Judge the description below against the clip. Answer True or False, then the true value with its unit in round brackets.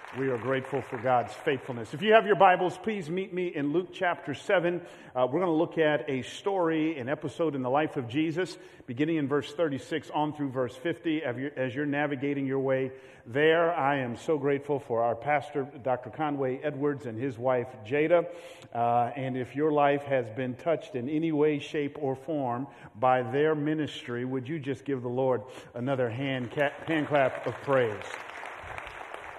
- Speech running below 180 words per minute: False (185 wpm)